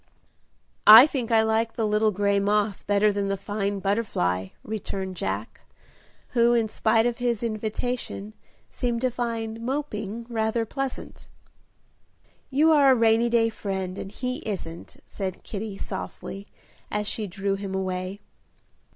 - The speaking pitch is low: No, high, 215 Hz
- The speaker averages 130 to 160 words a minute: Yes, average, 140 wpm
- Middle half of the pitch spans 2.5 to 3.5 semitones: Yes, average, 2.9 semitones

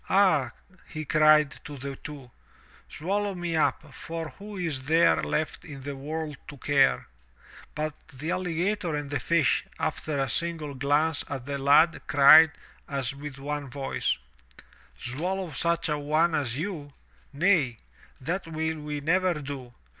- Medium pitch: Yes, medium, 150 Hz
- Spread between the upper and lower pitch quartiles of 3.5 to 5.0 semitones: No, average, 3.0 semitones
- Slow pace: No, average, 145 wpm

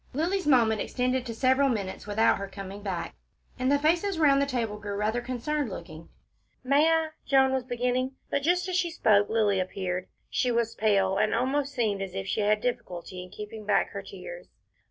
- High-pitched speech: Yes, high, 235 Hz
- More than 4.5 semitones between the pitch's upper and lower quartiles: Yes, wide, 5.4 semitones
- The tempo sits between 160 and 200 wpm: Yes, average, 195 wpm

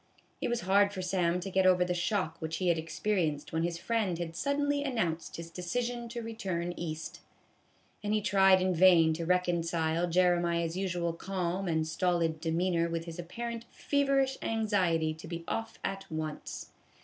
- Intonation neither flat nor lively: Yes, average, 3.3 semitones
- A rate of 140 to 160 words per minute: No, average, 175 wpm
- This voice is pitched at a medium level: Yes, medium, 180 Hz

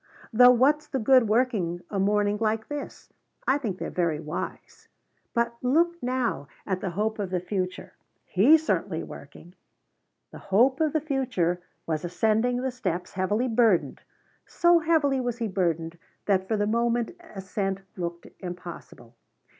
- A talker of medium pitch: No, high, 215 Hz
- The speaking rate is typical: Yes, average, 150 wpm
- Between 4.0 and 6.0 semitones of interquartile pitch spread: Yes, wide, 5.6 semitones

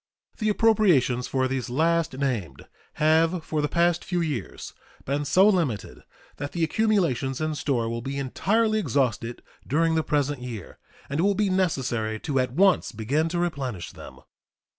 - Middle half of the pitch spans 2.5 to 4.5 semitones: No, wide, 5.4 semitones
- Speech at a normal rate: Yes, average, 160 wpm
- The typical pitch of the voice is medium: Yes, medium, 145 Hz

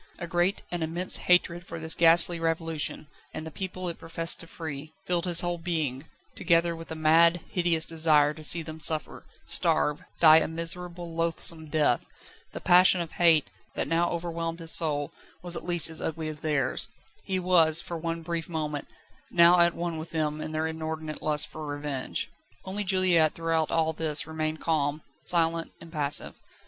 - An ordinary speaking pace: Yes, average, 175 wpm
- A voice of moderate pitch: Yes, medium, 165 Hz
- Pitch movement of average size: No, narrow, 1.6 semitones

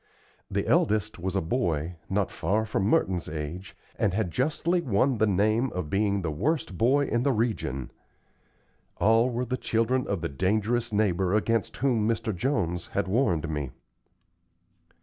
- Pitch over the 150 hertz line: No, low, 105 Hz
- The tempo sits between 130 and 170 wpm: Yes, average, 155 wpm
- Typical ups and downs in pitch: Yes, average, 4.8 semitones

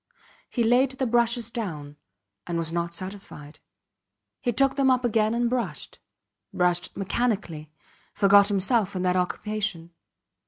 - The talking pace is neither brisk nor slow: No, slow, 130 wpm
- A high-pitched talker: Yes, high, 205 Hz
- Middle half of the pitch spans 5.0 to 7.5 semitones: Yes, average, 5.3 semitones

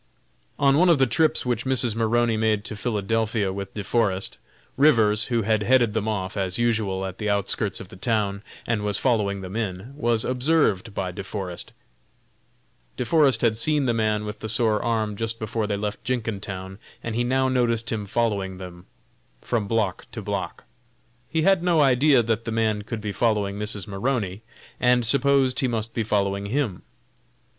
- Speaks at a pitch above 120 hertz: No, low, 110 Hz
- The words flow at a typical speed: Yes, average, 180 wpm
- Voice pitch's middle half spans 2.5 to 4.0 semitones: Yes, average, 3.1 semitones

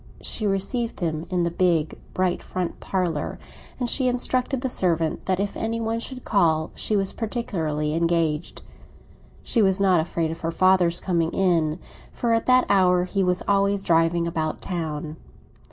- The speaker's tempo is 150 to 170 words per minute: Yes, average, 165 wpm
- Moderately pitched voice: Yes, medium, 180 Hz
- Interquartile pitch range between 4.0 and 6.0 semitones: No, average, 3.6 semitones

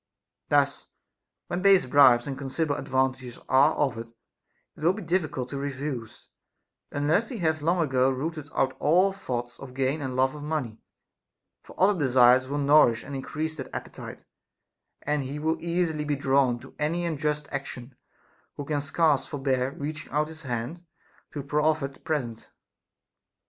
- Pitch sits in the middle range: Yes, medium, 145 Hz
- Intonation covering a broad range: No, average, 3.2 semitones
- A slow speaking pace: No, average, 160 wpm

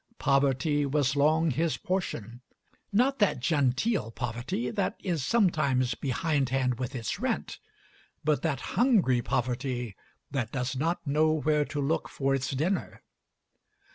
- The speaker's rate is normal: No, slow, 130 wpm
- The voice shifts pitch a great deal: No, average, 3.8 semitones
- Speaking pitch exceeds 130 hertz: Yes, medium, 140 Hz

